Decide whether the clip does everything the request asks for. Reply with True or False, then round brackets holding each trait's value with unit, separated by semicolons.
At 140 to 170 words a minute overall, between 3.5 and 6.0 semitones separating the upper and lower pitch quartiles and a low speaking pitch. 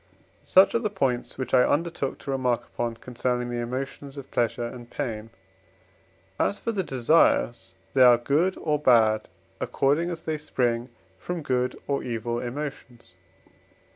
True (150 wpm; 3.8 semitones; 130 Hz)